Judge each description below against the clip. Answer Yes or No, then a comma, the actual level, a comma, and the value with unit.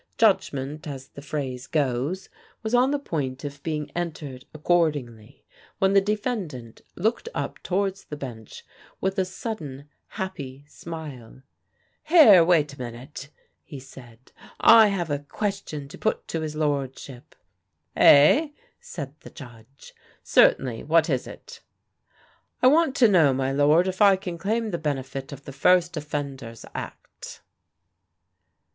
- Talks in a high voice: No, medium, 150 Hz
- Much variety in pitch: Yes, wide, 5.9 semitones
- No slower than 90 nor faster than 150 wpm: Yes, average, 140 wpm